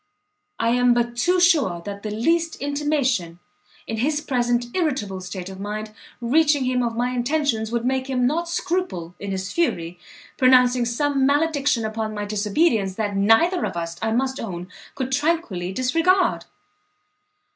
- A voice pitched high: Yes, high, 245 Hz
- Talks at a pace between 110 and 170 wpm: Yes, average, 155 wpm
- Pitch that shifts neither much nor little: No, wide, 5.8 semitones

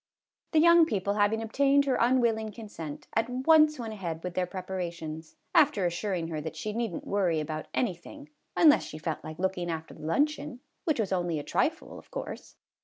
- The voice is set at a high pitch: Yes, high, 205 Hz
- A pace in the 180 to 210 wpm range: Yes, average, 190 wpm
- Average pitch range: No, wide, 7.4 semitones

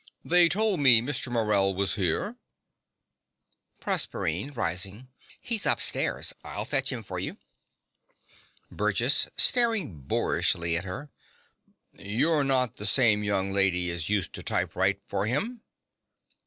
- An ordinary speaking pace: No, slow, 120 wpm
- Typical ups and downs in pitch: No, wide, 6.9 semitones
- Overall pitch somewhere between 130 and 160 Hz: No, low, 105 Hz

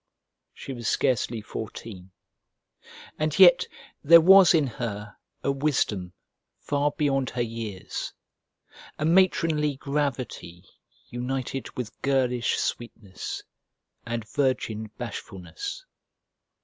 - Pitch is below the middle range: Yes, low, 130 Hz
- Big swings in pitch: No, average, 4.9 semitones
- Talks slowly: Yes, slow, 95 wpm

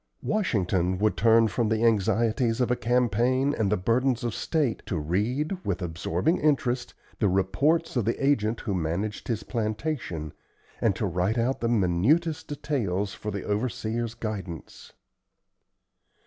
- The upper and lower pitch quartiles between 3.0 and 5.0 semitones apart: Yes, average, 4.3 semitones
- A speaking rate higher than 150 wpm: No, average, 145 wpm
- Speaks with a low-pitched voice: Yes, low, 110 Hz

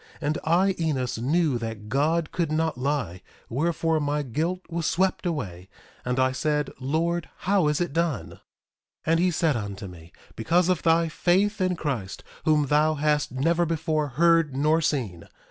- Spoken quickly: No, average, 175 wpm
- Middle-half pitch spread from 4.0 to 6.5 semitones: Yes, average, 4.3 semitones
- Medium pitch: Yes, medium, 155 Hz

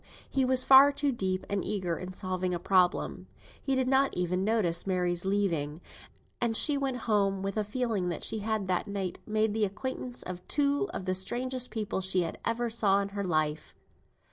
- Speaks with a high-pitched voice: Yes, high, 200 Hz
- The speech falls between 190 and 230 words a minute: Yes, average, 195 wpm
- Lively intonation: No, average, 4.7 semitones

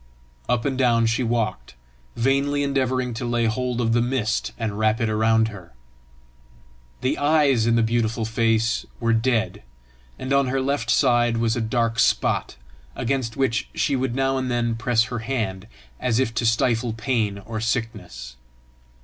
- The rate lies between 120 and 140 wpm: No, average, 165 wpm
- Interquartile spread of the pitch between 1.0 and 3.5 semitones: Yes, narrow, 2.4 semitones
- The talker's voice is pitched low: Yes, low, 115 Hz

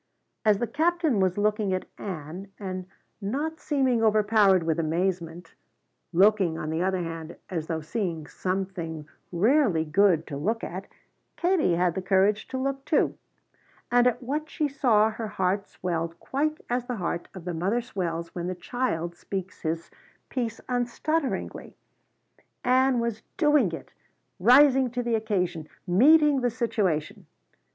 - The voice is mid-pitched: No, high, 200 Hz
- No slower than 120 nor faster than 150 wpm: Yes, average, 145 wpm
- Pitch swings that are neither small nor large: No, wide, 6.1 semitones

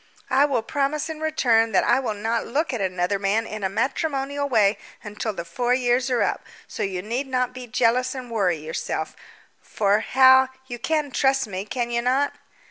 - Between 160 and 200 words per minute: Yes, average, 195 wpm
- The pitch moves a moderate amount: Yes, average, 4.0 semitones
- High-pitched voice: Yes, high, 245 Hz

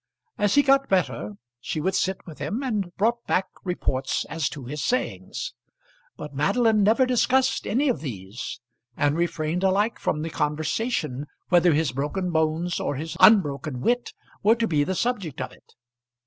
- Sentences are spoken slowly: No, average, 165 wpm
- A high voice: No, medium, 175 Hz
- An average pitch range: No, wide, 6.9 semitones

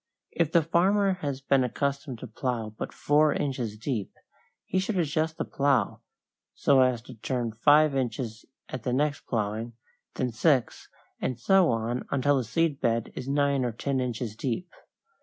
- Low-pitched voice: Yes, low, 130 Hz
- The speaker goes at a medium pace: Yes, average, 165 wpm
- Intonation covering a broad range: No, average, 3.9 semitones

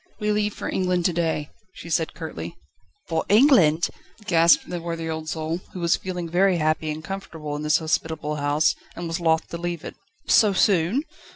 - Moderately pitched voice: Yes, medium, 165 Hz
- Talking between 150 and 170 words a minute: No, average, 185 wpm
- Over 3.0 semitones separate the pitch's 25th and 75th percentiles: No, narrow, 2.4 semitones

